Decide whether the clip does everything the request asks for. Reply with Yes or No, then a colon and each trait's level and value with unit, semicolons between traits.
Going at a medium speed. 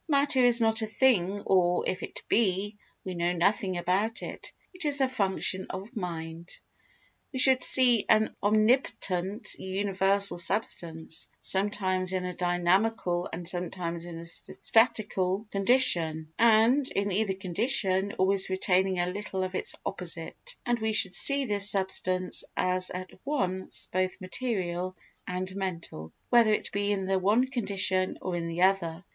Yes: average, 150 wpm